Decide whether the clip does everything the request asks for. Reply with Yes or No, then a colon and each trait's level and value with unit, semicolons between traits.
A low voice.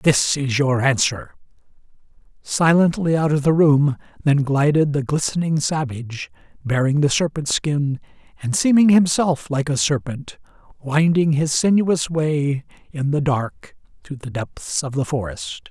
No: medium, 145 Hz